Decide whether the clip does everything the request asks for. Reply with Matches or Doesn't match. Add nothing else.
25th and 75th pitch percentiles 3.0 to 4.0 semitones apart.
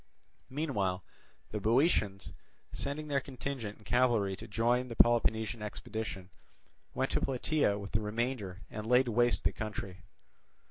Matches